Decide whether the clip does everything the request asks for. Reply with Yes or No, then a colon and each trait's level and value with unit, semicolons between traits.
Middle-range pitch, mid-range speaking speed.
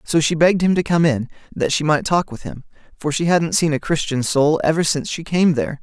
No: medium, 155 Hz; fast, 260 wpm